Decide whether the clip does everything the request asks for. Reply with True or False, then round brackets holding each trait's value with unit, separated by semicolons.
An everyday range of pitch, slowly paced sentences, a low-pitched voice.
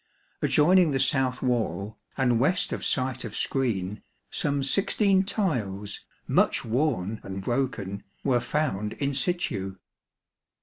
False (6.1 semitones; 120 wpm; 130 Hz)